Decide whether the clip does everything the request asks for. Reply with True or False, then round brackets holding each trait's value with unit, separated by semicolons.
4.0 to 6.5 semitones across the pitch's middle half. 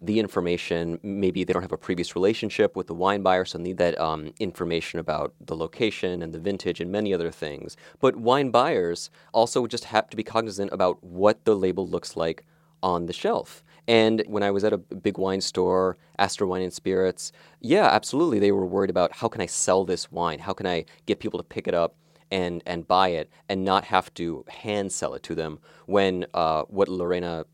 False (2.6 semitones)